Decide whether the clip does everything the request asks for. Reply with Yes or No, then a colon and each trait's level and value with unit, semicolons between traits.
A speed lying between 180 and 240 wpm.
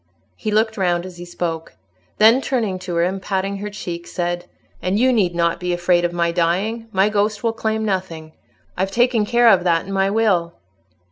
Yes: average, 200 wpm